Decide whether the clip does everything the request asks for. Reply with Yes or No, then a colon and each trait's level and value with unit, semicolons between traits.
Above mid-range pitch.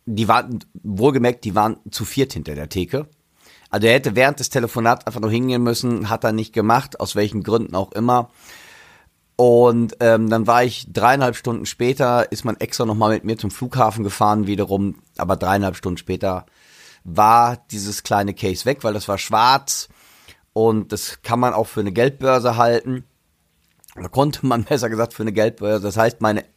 No: low, 110 Hz